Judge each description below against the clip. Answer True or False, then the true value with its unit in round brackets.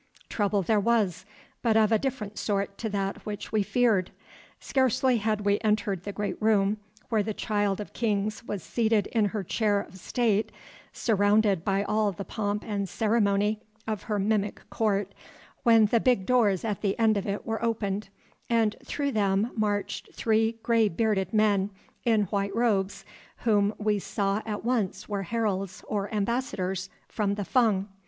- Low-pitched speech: False (210 Hz)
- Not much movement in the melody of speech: True (1.9 semitones)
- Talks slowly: False (165 wpm)